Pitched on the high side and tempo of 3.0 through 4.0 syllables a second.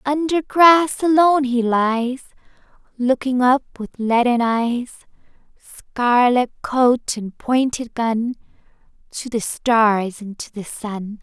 Yes: high, 245 Hz; 3.3 syllables/s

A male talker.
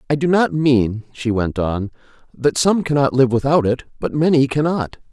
Yes: male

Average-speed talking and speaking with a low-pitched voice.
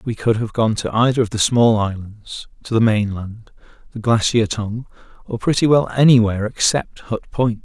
Yes: average, 180 wpm; low, 110 Hz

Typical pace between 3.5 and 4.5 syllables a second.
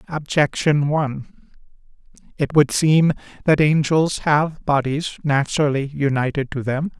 Yes: 4.4 syllables/s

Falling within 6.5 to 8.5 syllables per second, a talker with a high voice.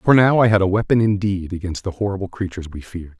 No: 6.8 syllables/s; very low, 95 Hz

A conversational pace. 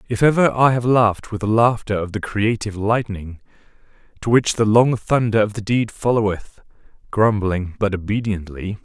Yes: average, 165 wpm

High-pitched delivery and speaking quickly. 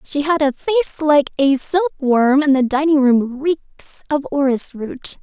No: very high, 285 Hz; average, 170 wpm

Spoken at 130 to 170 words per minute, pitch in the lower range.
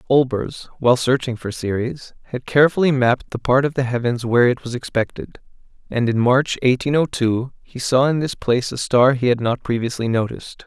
No: average, 195 wpm; low, 125 Hz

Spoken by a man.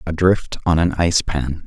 Yes: male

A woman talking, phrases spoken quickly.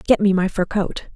Yes: female; fast, 260 wpm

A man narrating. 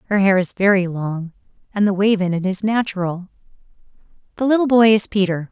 No: female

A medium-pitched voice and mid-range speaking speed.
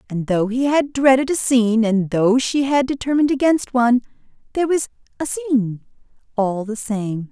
No: high, 245 Hz; average, 170 wpm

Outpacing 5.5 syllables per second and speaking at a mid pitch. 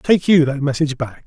Yes: 5.7 syllables/s; medium, 145 Hz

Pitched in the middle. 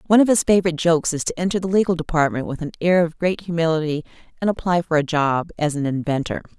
Yes: medium, 165 Hz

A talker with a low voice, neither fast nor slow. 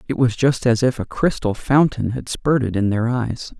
No: low, 120 Hz; fast, 215 wpm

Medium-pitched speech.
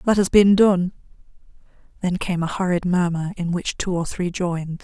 Yes: medium, 180 Hz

